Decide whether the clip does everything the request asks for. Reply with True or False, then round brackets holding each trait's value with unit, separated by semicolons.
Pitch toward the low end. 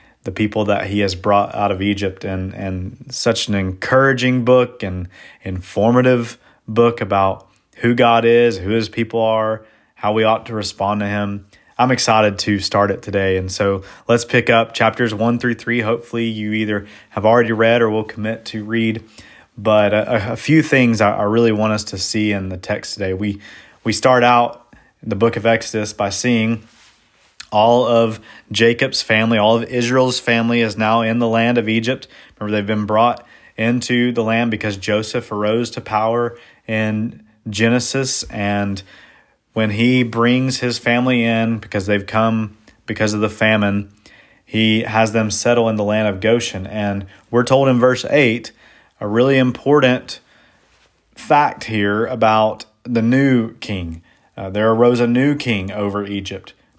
True (110 Hz)